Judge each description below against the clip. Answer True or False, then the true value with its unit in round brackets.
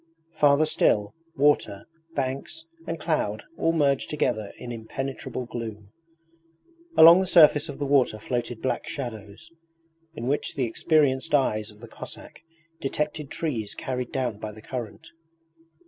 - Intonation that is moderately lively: True (4.8 semitones)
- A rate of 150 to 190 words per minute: False (135 wpm)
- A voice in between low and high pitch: False (130 Hz)